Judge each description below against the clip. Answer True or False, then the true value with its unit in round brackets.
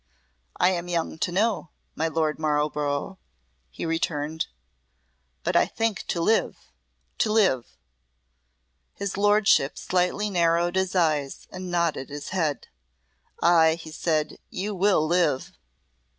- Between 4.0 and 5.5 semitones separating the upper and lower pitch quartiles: False (3.4 semitones)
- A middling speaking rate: False (120 wpm)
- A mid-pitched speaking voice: True (170 Hz)